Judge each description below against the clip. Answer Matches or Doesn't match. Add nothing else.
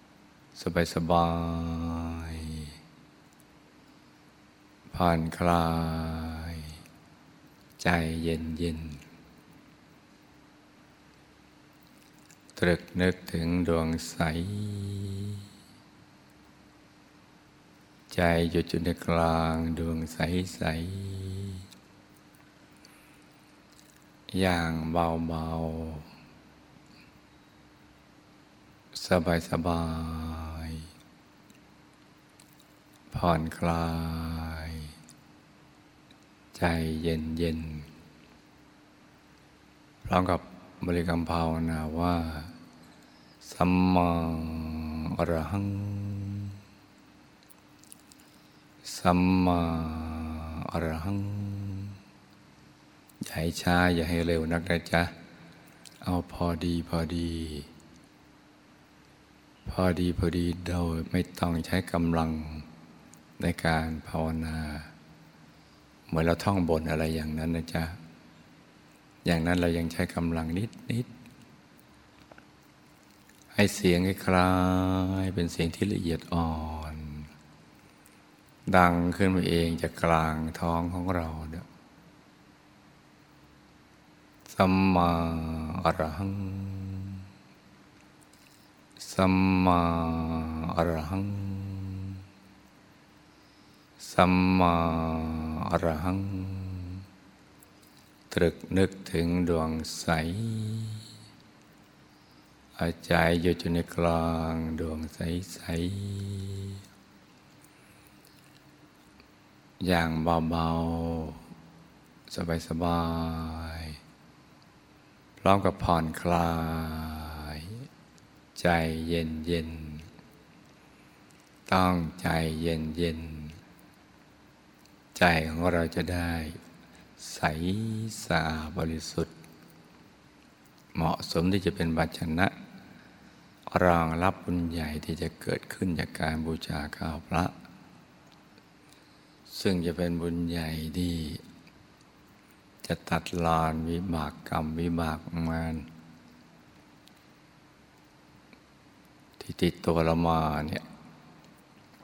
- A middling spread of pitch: Doesn't match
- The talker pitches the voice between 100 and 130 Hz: Doesn't match